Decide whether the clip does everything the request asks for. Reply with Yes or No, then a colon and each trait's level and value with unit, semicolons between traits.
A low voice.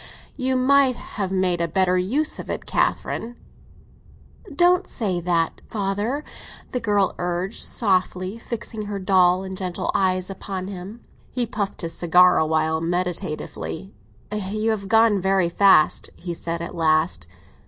No: high, 190 Hz